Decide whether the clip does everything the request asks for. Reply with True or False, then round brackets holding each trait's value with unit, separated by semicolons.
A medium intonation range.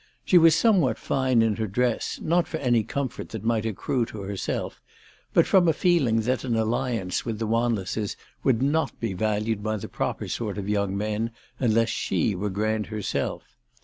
True (3.5 semitones)